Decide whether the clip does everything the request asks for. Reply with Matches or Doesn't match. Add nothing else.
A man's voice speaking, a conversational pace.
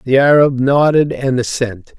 Matches